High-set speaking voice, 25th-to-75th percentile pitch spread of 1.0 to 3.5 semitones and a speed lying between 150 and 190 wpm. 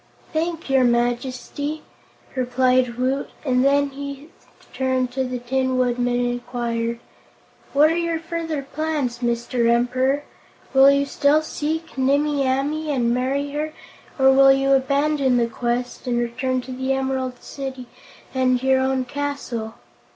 No: very high, 265 Hz; narrow, 2.4 semitones; average, 140 wpm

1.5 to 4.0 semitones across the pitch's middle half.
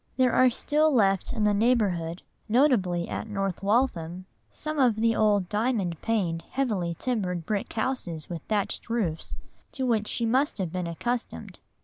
No: average, 5.3 semitones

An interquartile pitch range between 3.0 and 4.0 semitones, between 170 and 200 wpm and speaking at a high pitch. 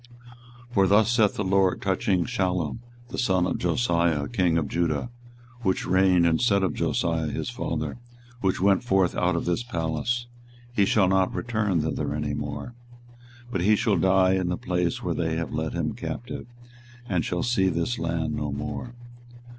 No: average, 3.5 semitones; average, 175 wpm; very low, 95 Hz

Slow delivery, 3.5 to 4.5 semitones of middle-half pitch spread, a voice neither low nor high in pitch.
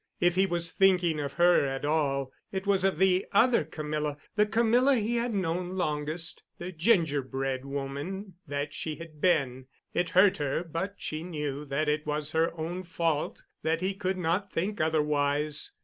No: average, 165 wpm; average, 4.0 semitones; medium, 165 Hz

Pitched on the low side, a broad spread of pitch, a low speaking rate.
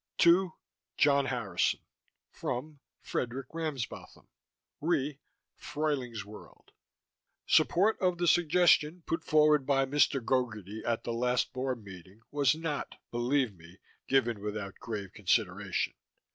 Yes: low, 130 Hz; wide, 5.7 semitones; slow, 115 wpm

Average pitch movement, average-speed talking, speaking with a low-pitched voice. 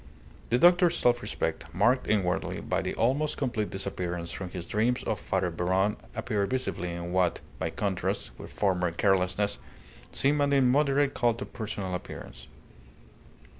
No: wide, 5.8 semitones; average, 145 wpm; low, 100 Hz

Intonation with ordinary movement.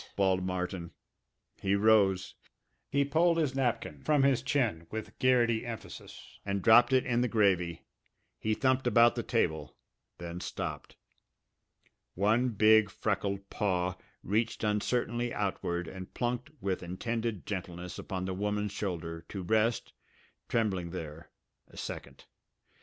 Yes: average, 4.4 semitones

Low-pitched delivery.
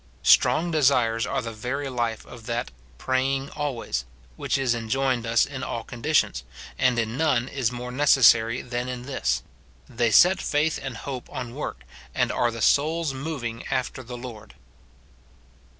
Yes: low, 125 Hz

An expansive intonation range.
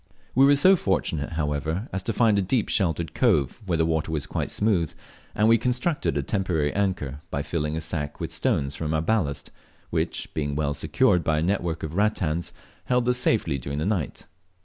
Yes: wide, 5.8 semitones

